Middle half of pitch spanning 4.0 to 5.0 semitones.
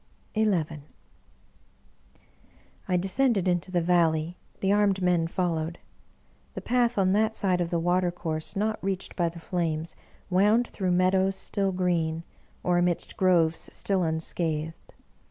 No: narrow, 2.6 semitones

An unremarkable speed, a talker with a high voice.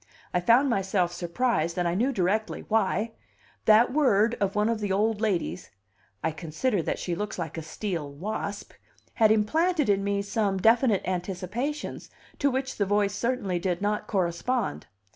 Yes: average, 160 wpm; high, 205 Hz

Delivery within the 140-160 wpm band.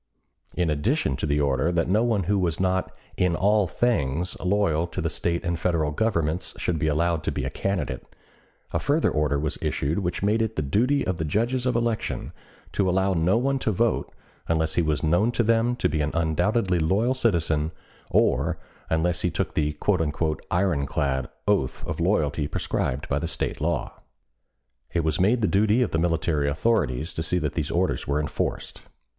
No: average, 190 wpm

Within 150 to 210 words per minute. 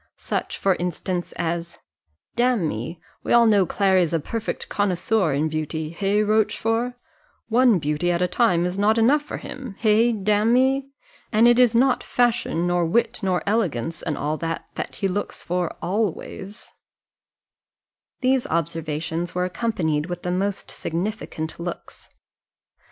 No: average, 140 wpm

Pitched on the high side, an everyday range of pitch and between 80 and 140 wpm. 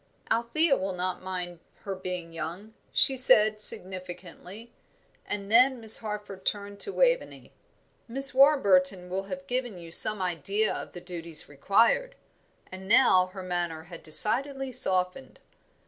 Yes: high, 195 Hz; average, 4.3 semitones; slow, 135 wpm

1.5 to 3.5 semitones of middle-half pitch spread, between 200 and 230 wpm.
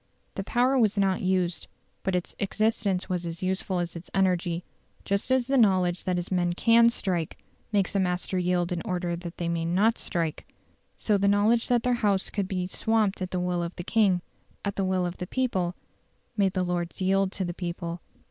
Yes: narrow, 2.4 semitones; fast, 205 wpm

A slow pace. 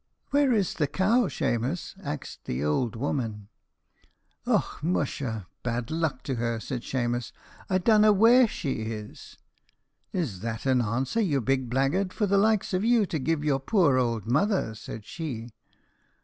No: average, 155 wpm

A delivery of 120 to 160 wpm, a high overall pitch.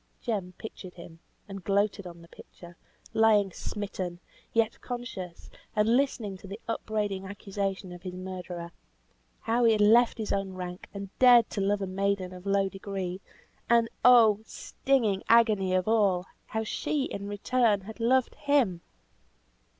Yes: average, 150 wpm; high, 200 Hz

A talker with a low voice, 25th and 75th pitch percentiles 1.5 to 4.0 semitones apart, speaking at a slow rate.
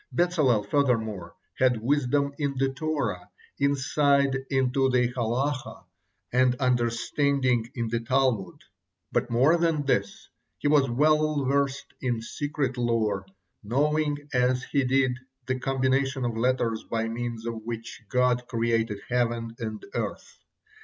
Yes: low, 125 Hz; average, 3.2 semitones; slow, 125 wpm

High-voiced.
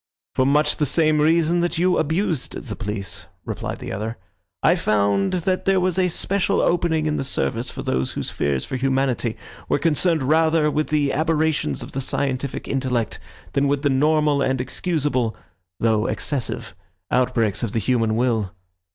No: medium, 140 Hz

